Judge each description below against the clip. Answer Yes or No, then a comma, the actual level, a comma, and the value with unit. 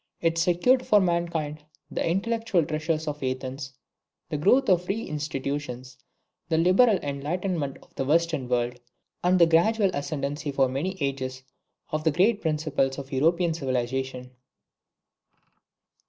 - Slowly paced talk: Yes, slow, 130 wpm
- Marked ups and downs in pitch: No, average, 4.6 semitones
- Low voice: No, medium, 155 Hz